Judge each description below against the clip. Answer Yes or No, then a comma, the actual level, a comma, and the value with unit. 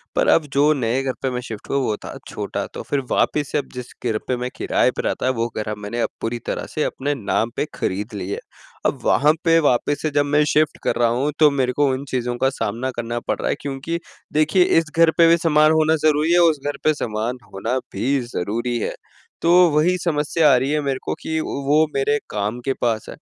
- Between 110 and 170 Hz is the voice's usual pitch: Yes, low, 135 Hz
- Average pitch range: Yes, average, 4.2 semitones